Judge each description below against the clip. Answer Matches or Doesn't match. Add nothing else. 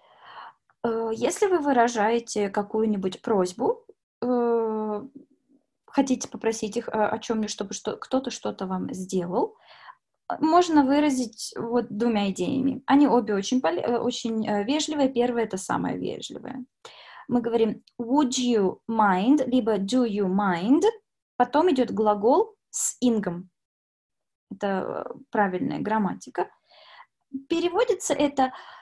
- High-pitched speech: Matches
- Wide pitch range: Doesn't match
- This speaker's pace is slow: Matches